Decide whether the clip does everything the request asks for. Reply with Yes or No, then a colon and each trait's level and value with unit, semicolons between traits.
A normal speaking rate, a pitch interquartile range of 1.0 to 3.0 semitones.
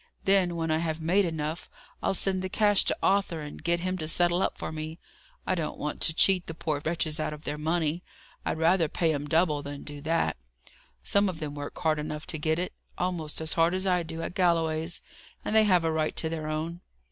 No: fast, 230 wpm; narrow, 2.5 semitones